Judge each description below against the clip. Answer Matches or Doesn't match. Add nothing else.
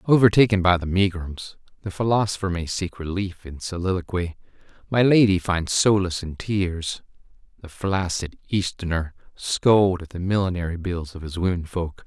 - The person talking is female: Doesn't match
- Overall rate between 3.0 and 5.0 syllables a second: Matches